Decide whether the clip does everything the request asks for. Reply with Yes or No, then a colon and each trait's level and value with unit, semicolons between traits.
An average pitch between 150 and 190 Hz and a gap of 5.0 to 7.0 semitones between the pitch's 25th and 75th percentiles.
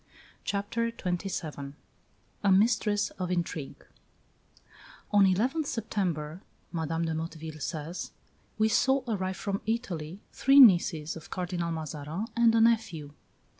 Yes: medium, 185 Hz; average, 5.3 semitones